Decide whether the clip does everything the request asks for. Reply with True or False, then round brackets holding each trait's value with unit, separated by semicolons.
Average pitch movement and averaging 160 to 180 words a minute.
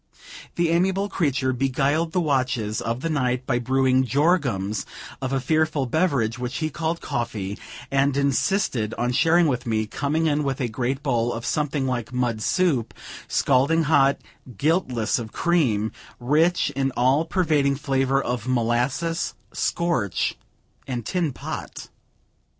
False (4.4 semitones; 145 wpm)